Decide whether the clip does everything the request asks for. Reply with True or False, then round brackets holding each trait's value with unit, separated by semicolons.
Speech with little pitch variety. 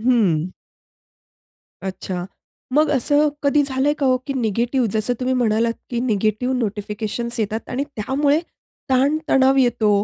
False (3.7 semitones)